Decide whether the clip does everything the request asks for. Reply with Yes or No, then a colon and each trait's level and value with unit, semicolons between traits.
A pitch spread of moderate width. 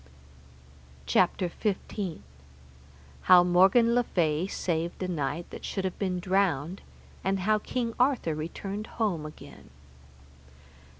Yes: average, 3.5 semitones